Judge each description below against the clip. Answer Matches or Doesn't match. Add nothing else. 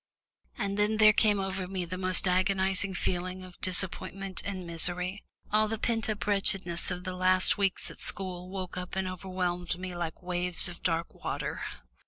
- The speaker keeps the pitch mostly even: Matches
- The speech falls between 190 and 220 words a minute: Doesn't match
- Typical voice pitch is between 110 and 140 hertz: Doesn't match